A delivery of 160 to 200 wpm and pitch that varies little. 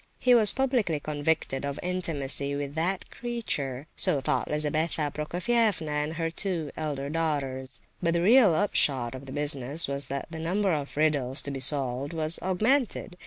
No: average, 165 wpm; average, 4.4 semitones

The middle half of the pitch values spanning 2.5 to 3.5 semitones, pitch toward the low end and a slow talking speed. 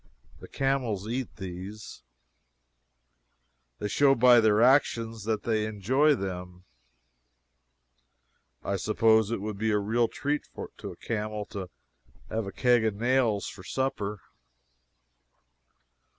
Yes: average, 3.1 semitones; low, 110 Hz; slow, 120 wpm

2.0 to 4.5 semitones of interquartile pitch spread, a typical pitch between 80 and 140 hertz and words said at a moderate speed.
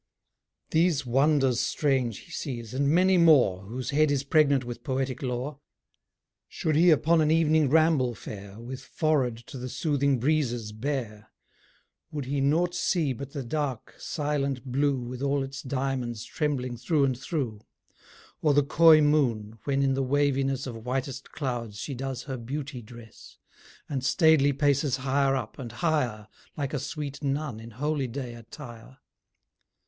Yes: average, 3.2 semitones; low, 135 Hz; average, 155 wpm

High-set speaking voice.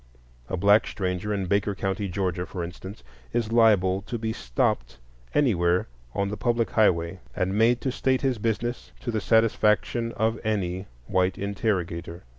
No: low, 100 Hz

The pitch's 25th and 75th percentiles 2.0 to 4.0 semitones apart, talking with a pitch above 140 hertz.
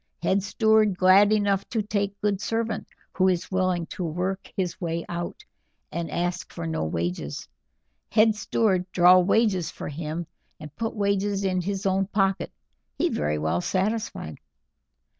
Yes: average, 2.9 semitones; high, 190 Hz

